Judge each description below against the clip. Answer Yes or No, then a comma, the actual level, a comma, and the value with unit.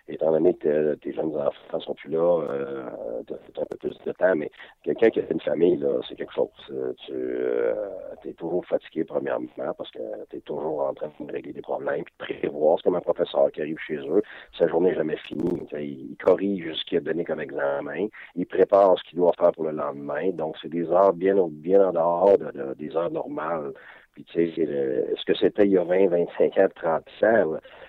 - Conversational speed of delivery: No, fast, 230 wpm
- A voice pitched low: No, very high, 395 Hz